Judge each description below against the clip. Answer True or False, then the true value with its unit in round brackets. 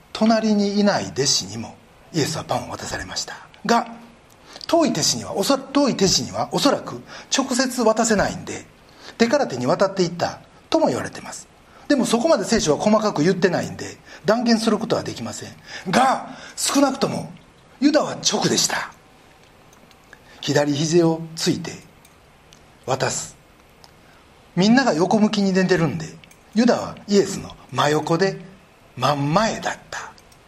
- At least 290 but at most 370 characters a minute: True (295 characters per minute)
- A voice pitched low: False (205 Hz)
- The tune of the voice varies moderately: False (6.1 semitones)